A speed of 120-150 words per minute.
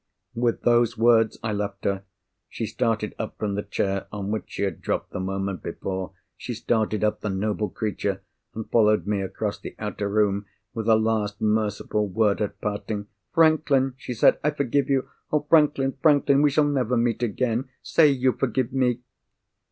No: average, 170 wpm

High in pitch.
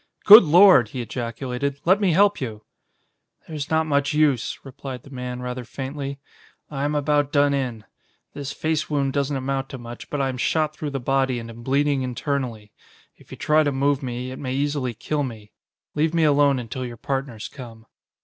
No: low, 135 Hz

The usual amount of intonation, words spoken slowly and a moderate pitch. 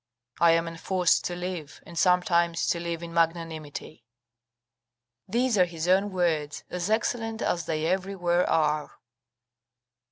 No: narrow, 1.9 semitones; slow, 130 wpm; medium, 170 Hz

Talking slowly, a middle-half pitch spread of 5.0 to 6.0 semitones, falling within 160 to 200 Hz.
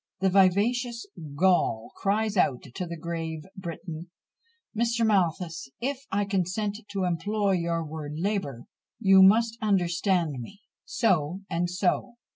No: slow, 125 wpm; average, 3.7 semitones; high, 190 Hz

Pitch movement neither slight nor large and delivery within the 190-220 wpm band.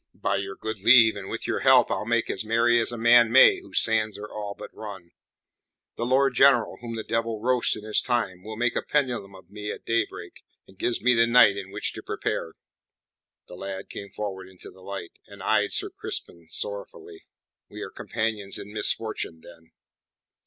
Yes: average, 3.1 semitones; average, 195 wpm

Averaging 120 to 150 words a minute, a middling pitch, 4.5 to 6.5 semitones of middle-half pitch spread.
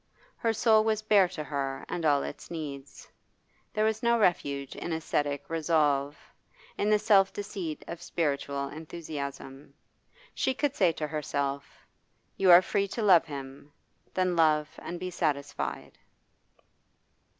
Yes: average, 140 wpm; medium, 160 Hz; wide, 5.4 semitones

